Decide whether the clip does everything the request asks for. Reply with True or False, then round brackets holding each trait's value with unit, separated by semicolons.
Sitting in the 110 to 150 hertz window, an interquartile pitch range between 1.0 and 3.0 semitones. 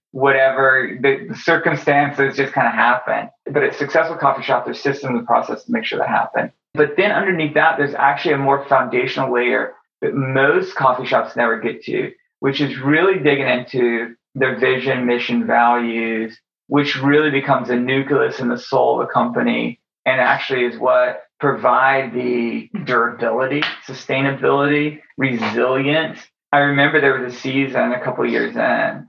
True (135 Hz; 2.5 semitones)